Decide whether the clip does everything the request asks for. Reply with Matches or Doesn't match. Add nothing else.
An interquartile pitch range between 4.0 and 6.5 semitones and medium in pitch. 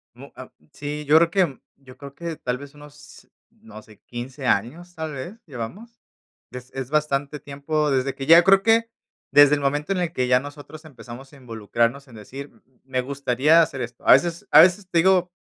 Matches